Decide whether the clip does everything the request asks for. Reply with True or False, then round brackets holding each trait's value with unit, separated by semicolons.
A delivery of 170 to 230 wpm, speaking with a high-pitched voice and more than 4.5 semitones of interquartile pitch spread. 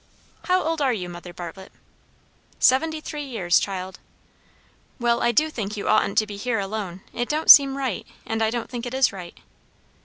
True (185 wpm; 230 Hz; 5.6 semitones)